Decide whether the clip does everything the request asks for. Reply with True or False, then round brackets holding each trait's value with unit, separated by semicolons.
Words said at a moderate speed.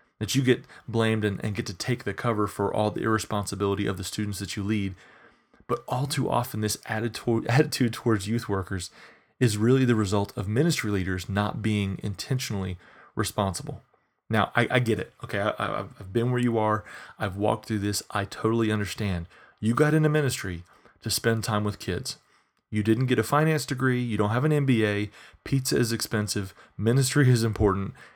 True (185 wpm)